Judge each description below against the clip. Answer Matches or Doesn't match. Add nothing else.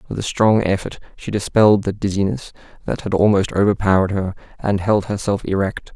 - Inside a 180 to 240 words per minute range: Doesn't match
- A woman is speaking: Doesn't match